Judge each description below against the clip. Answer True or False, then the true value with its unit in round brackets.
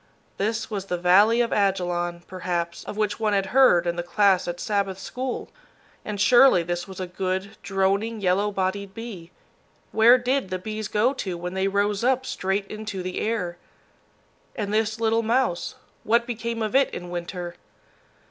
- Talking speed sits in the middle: True (170 wpm)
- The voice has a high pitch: True (200 Hz)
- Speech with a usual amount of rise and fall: True (3.5 semitones)